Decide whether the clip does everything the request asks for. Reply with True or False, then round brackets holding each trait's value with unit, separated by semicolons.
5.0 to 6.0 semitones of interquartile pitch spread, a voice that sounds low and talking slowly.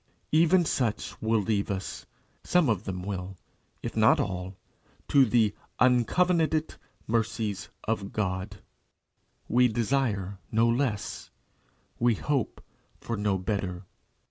False (4.0 semitones; 110 Hz; 115 wpm)